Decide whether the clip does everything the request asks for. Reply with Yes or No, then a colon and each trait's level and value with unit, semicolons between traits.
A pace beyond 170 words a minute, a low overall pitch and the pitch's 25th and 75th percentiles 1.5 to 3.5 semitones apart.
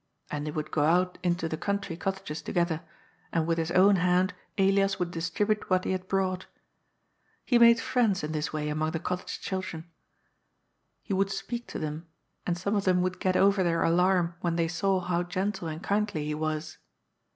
No: average, 190 wpm; medium, 180 Hz; average, 3.0 semitones